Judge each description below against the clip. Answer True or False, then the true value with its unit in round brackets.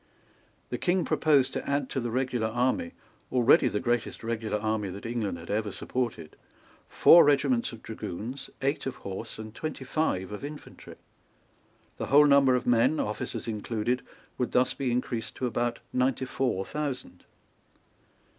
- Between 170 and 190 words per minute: False (155 wpm)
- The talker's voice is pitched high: False (125 Hz)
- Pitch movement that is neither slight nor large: True (3.6 semitones)